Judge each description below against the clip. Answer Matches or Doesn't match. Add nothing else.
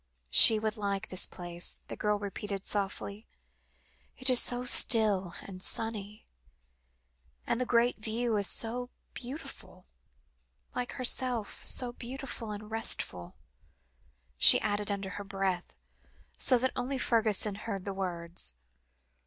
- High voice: Matches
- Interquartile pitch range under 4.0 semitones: Matches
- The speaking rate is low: Matches